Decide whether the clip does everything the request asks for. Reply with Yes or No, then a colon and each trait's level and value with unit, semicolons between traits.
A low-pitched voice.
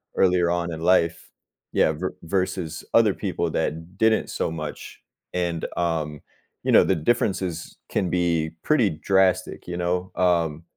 Yes: very low, 85 Hz